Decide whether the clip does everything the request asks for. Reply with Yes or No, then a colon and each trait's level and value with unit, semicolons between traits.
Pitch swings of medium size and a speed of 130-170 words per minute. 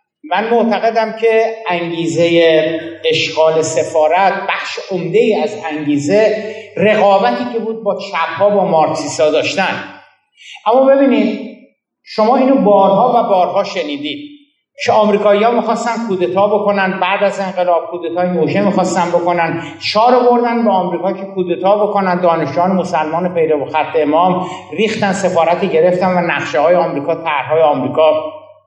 No: average, 4.6 semitones; average, 120 wpm